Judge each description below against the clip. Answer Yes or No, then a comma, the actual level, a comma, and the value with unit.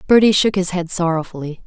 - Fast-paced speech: No, average, 180 wpm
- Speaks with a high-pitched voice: No, medium, 180 Hz